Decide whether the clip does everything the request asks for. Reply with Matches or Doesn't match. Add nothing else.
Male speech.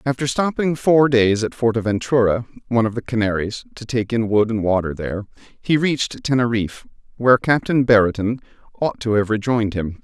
Matches